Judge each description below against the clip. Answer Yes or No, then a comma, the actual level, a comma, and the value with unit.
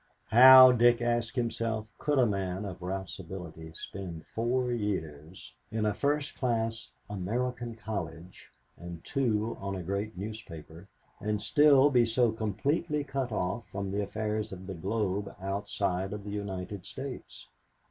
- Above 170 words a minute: No, average, 145 wpm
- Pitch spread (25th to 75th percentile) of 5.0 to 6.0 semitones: No, average, 3.9 semitones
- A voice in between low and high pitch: No, low, 105 Hz